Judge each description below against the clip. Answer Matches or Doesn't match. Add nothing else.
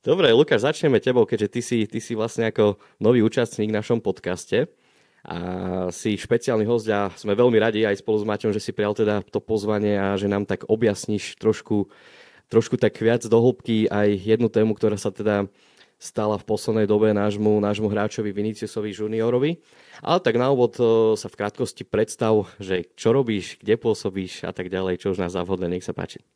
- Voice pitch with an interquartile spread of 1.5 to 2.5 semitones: Matches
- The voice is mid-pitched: Doesn't match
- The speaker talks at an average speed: Doesn't match